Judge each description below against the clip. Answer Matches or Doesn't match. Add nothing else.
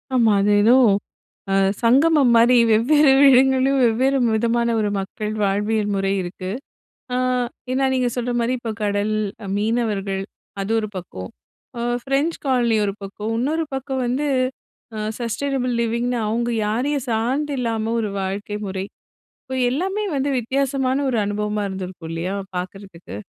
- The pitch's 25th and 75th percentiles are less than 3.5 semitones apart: Doesn't match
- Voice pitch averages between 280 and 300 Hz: Doesn't match